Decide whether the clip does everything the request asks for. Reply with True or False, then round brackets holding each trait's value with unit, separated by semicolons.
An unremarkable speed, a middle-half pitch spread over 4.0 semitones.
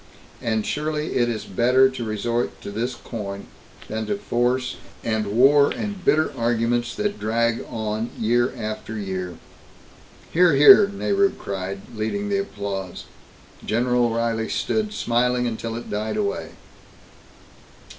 False (130 wpm; 4.6 semitones)